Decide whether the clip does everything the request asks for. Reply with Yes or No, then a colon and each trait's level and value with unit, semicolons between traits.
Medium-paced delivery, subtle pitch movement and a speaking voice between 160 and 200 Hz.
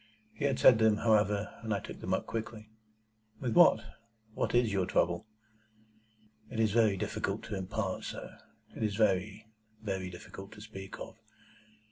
No: average, 160 wpm; narrow, 2.3 semitones; low, 105 Hz